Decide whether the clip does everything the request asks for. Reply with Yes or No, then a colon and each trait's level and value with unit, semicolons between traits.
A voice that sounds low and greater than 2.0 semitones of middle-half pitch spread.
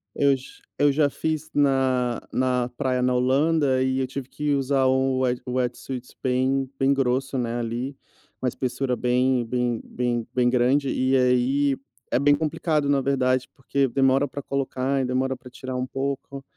No: low, 130 Hz; narrow, 1.5 semitones